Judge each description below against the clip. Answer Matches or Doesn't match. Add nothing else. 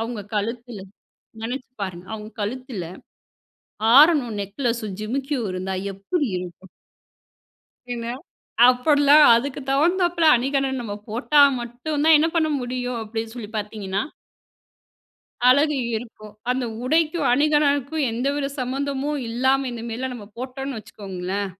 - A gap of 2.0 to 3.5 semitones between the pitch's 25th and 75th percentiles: Doesn't match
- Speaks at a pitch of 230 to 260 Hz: Matches